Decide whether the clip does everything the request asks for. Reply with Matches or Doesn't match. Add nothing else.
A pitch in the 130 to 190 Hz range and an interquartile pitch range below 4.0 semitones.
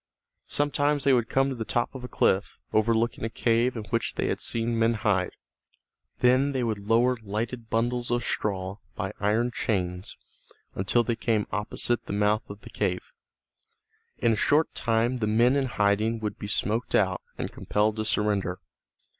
Doesn't match